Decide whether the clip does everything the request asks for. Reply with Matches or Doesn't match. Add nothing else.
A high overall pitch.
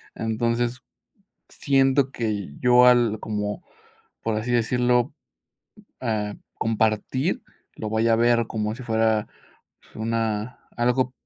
Doesn't match